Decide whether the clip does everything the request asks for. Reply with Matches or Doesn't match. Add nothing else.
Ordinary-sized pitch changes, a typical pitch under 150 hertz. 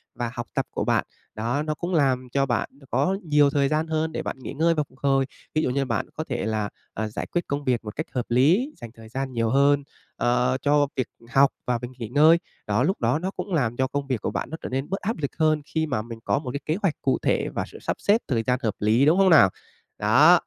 Matches